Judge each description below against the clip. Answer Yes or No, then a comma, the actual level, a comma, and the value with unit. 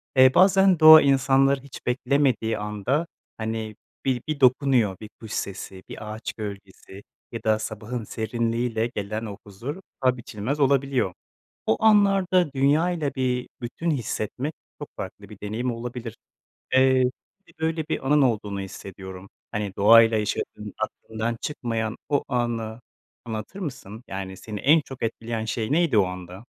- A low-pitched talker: Yes, low, 120 Hz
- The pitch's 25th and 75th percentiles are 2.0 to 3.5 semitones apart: No, average, 4.3 semitones